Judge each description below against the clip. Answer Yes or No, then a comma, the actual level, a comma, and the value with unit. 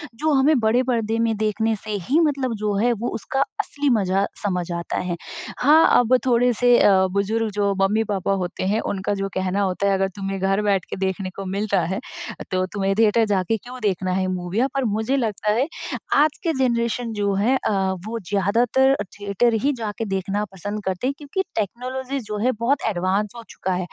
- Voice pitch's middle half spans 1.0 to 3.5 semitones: No, average, 4.0 semitones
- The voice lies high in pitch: Yes, high, 210 Hz